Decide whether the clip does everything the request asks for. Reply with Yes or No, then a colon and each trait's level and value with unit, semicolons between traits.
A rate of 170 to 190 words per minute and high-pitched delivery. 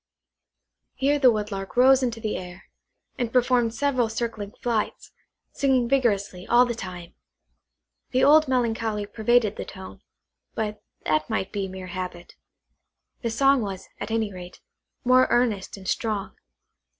No: average, 140 wpm; high, 225 Hz